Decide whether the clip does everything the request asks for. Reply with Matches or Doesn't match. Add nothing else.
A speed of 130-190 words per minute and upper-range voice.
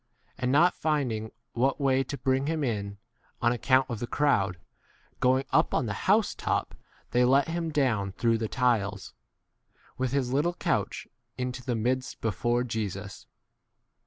Doesn't match